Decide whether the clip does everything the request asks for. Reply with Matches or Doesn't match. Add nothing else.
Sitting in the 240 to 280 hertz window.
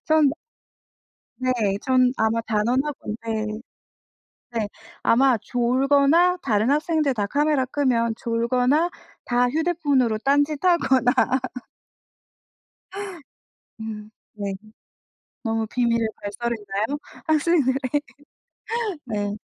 Matches